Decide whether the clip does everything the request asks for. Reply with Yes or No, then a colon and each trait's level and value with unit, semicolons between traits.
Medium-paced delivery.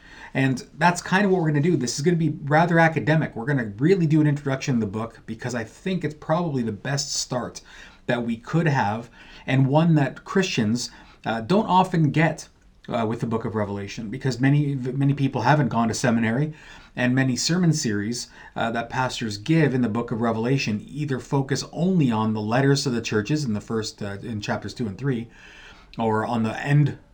No: fast, 210 wpm